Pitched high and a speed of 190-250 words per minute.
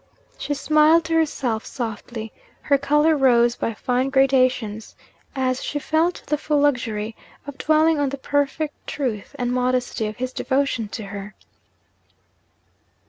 No: very high, 265 Hz; average, 140 wpm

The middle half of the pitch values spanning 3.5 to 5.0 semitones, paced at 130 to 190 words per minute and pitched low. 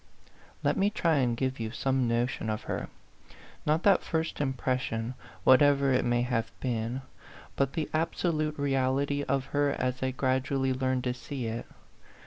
No: narrow, 2.5 semitones; average, 155 wpm; low, 130 Hz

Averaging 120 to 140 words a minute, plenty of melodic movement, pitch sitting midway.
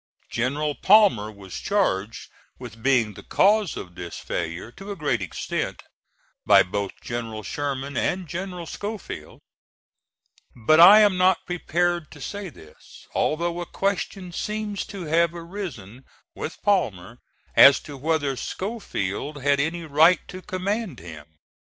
Yes: slow, 135 wpm; wide, 7.9 semitones; medium, 155 Hz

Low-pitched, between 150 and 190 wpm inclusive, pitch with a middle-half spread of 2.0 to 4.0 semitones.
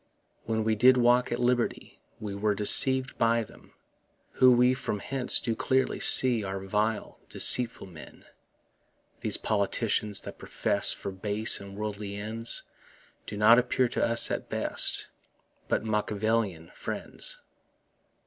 No: low, 110 Hz; slow, 135 wpm; average, 3.0 semitones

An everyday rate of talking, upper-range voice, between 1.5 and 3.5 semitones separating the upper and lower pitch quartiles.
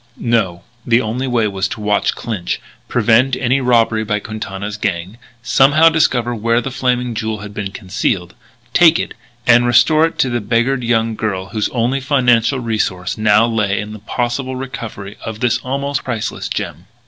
No: average, 170 wpm; low, 115 Hz; average, 3.2 semitones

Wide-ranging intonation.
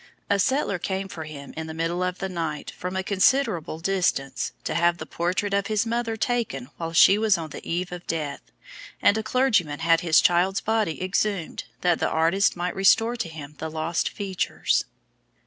No: average, 3.7 semitones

